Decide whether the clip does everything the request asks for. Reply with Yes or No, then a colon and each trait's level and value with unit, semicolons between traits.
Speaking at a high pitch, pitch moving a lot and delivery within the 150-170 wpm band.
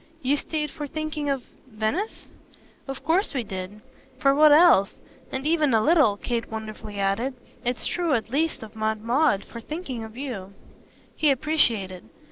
Yes: very high, 260 Hz; wide, 5.8 semitones; average, 160 wpm